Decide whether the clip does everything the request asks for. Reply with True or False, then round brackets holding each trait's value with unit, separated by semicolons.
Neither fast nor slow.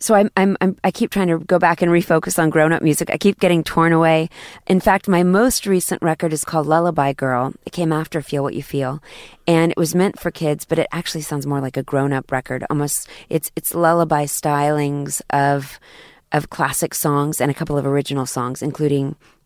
False (215 wpm)